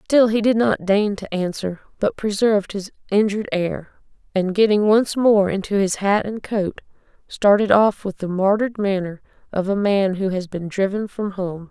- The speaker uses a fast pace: No, average, 185 wpm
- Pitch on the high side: Yes, high, 200 Hz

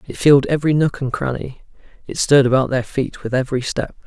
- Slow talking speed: No, fast, 205 wpm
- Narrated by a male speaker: Yes, male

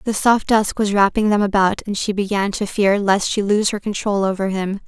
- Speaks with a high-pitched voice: Yes, high, 205 Hz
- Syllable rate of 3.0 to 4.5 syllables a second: No, 5.1 syllables/s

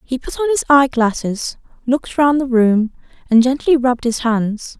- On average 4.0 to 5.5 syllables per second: Yes, 5.2 syllables/s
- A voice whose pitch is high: Yes, very high, 255 Hz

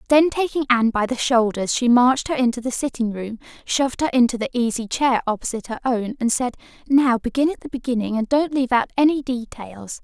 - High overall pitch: Yes, high, 245 Hz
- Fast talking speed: Yes, fast, 210 wpm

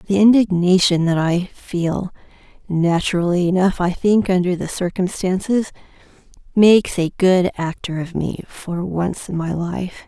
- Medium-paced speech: No, slow, 125 wpm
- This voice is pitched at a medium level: Yes, medium, 180 Hz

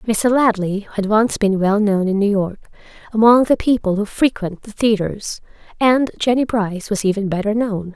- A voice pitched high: Yes, high, 210 Hz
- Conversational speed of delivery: Yes, average, 180 wpm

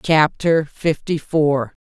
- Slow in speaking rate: Yes, slow, 100 wpm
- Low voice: No, medium, 155 Hz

